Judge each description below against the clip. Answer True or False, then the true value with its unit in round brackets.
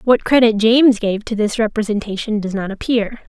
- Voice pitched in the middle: False (220 Hz)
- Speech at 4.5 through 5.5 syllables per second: True (5.4 syllables/s)